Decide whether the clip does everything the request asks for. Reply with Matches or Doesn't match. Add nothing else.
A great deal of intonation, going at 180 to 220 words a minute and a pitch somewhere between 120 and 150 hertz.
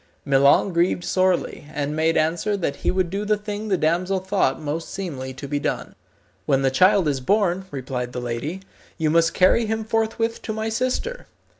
Doesn't match